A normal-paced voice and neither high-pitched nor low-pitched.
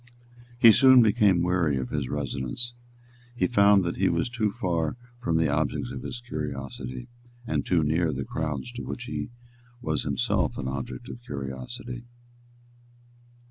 No: average, 155 wpm; very low, 85 Hz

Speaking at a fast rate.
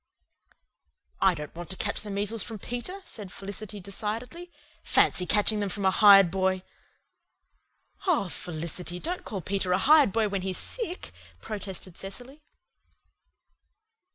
No: slow, 135 wpm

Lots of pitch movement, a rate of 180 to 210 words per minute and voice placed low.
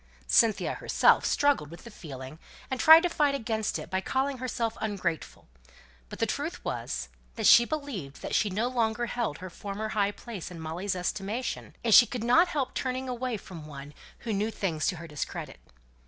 No: wide, 5.9 semitones; average, 185 wpm; high, 220 Hz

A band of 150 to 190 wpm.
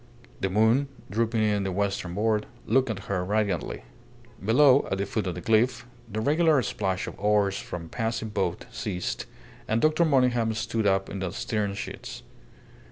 Yes: average, 170 wpm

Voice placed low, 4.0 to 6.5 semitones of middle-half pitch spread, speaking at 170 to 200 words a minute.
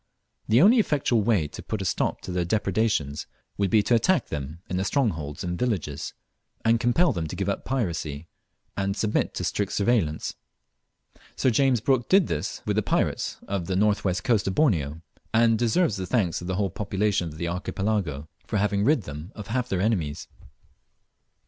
Yes: low, 100 Hz; average, 4.9 semitones; average, 185 wpm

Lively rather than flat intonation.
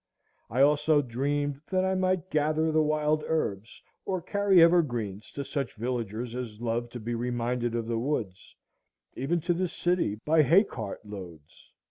Yes: wide, 5.7 semitones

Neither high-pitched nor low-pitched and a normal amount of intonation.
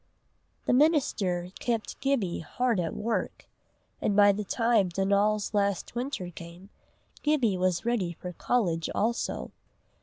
No: high, 205 Hz; average, 4.7 semitones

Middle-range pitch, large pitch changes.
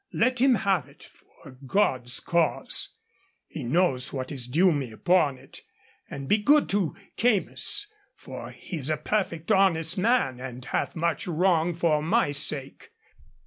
Yes: medium, 165 Hz; wide, 6.0 semitones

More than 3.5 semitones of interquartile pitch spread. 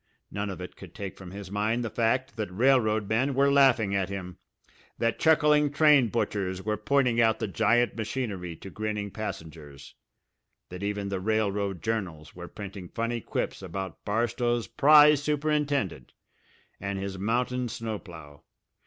Yes: average, 4.0 semitones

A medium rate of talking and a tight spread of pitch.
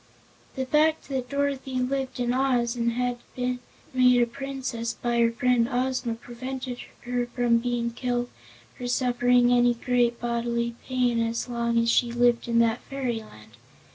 Yes: average, 160 wpm; narrow, 1.4 semitones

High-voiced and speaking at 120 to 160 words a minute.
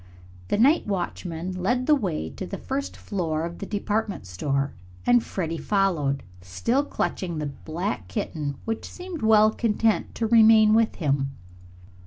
Yes: high, 195 Hz; average, 150 wpm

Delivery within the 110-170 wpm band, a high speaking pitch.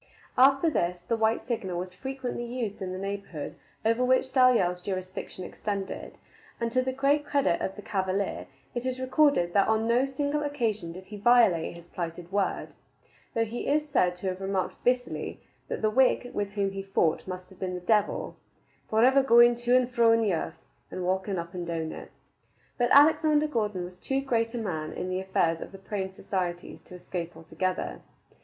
No: average, 190 wpm; high, 205 Hz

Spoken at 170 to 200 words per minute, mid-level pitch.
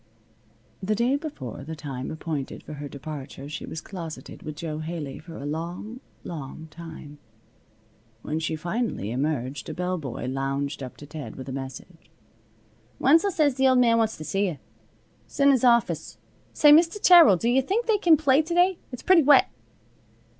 Yes: average, 175 wpm; medium, 165 Hz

